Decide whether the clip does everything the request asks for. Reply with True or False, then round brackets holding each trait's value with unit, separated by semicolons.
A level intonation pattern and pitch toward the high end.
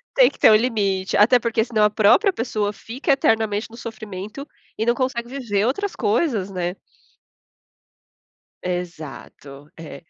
False (3.8 semitones; 220 Hz)